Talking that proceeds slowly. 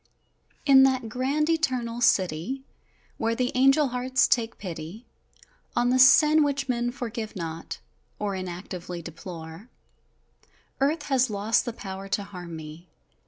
Yes: slow, 130 wpm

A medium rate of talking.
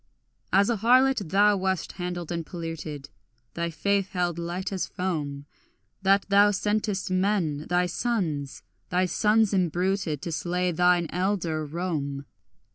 No: slow, 130 wpm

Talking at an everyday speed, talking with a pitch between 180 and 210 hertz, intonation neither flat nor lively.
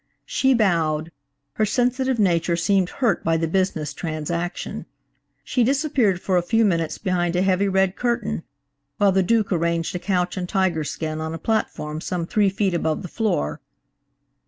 Yes: average, 165 wpm; medium, 185 Hz; average, 4.4 semitones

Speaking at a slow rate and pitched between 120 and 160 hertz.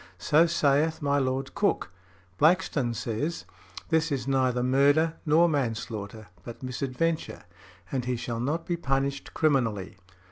Yes: slow, 130 wpm; low, 135 Hz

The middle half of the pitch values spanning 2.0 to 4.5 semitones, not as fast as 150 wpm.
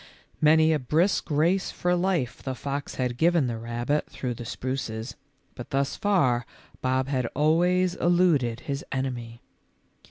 No: average, 5.3 semitones; average, 140 wpm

